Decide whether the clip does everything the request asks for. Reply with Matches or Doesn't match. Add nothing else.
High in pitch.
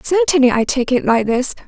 Matches